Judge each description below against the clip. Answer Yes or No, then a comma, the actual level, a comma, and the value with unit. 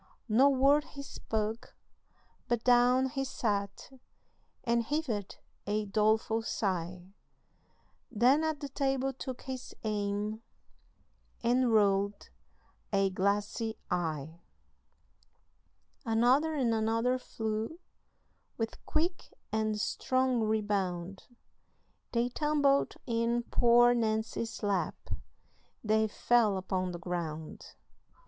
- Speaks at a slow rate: Yes, slow, 95 wpm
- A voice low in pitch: No, high, 225 Hz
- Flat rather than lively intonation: No, average, 3.7 semitones